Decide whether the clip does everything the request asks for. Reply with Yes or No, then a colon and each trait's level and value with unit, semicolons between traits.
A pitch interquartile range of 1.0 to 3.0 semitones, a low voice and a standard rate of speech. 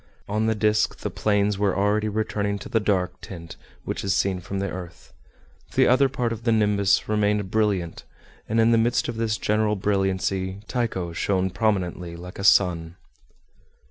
Yes: narrow, 2.4 semitones; low, 100 Hz; average, 175 wpm